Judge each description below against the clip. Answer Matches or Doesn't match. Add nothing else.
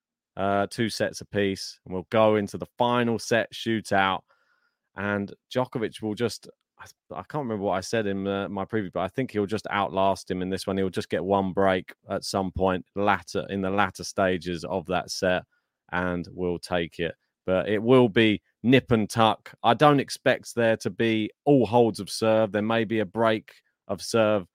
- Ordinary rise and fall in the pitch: Matches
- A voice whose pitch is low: Matches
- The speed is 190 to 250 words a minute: Matches